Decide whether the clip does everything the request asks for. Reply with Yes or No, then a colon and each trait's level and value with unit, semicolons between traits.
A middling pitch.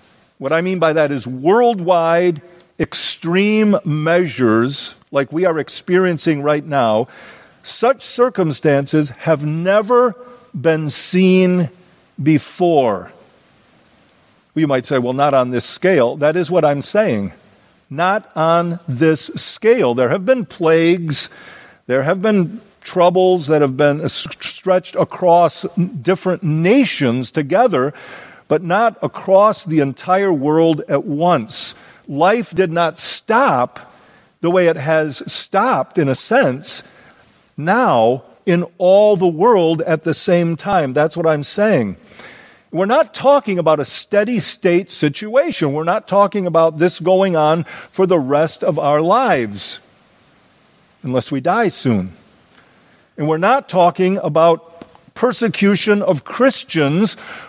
Yes: medium, 170 Hz